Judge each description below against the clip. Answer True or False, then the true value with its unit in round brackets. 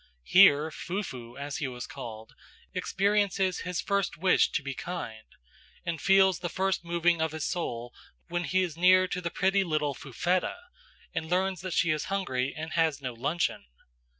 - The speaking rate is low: False (170 wpm)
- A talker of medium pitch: True (170 Hz)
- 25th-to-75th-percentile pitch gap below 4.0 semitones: False (4.5 semitones)